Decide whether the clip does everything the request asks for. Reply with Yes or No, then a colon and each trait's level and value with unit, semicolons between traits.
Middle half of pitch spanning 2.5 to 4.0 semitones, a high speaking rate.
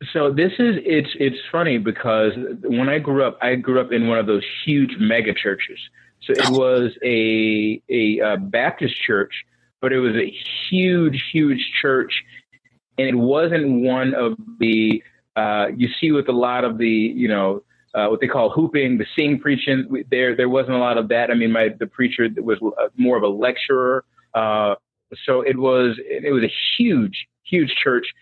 No: average, 3.4 semitones; average, 185 wpm